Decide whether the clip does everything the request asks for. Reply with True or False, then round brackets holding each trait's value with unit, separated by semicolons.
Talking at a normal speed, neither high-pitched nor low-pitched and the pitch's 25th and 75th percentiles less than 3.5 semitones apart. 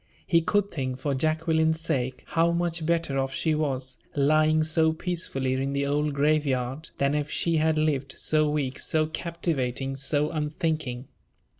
True (160 wpm; 150 Hz; 2.8 semitones)